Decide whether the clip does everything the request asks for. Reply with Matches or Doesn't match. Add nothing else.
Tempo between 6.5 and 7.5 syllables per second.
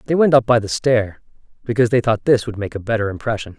Matches